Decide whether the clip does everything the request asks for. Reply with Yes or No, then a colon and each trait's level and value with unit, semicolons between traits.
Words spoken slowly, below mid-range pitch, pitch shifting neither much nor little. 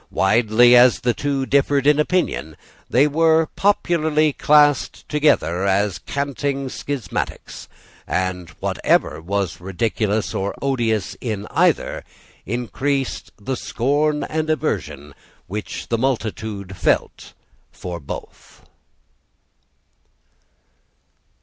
No: slow, 95 wpm; low, 125 Hz; wide, 6.3 semitones